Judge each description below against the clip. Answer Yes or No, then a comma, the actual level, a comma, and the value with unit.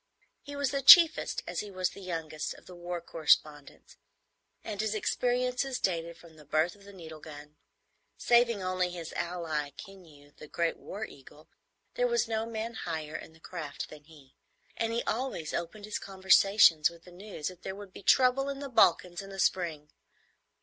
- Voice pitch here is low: No, medium, 185 Hz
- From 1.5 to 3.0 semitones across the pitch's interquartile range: No, wide, 5.4 semitones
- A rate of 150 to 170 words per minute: No, average, 185 wpm